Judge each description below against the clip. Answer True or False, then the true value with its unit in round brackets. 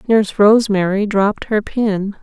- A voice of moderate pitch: False (205 Hz)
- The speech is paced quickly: False (135 wpm)